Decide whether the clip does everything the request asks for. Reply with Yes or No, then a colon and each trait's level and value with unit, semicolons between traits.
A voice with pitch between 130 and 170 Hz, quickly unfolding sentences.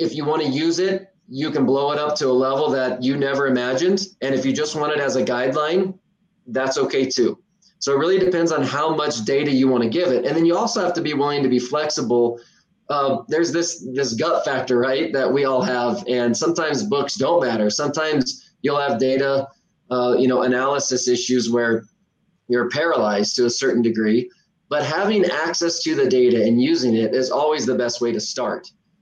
Yes: medium, 140 Hz; fast, 210 wpm